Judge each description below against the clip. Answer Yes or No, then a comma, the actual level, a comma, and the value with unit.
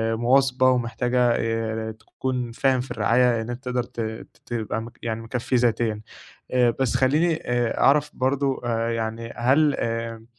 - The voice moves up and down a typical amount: No, narrow, 2.2 semitones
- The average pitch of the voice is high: No, low, 120 Hz